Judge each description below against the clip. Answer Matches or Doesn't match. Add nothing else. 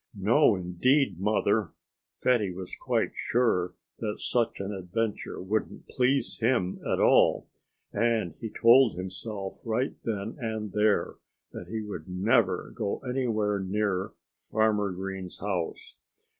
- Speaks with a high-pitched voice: Doesn't match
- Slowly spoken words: Matches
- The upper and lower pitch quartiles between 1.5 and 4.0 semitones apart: Matches